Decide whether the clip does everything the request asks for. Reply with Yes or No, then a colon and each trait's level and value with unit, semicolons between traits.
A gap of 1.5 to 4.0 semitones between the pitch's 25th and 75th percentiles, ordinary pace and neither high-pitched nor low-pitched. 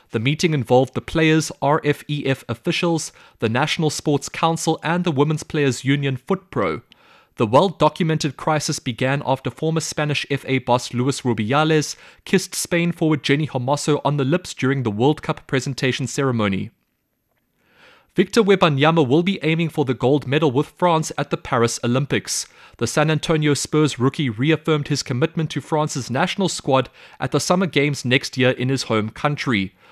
Yes: average, 3.2 semitones; average, 160 wpm; medium, 145 Hz